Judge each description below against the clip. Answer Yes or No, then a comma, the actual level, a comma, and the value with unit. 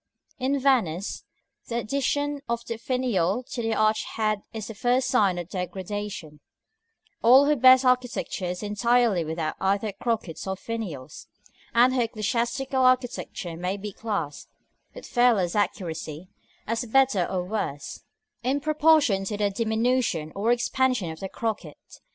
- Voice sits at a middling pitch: No, high, 220 Hz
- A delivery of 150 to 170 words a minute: No, average, 140 wpm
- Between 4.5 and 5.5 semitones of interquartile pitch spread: Yes, average, 4.8 semitones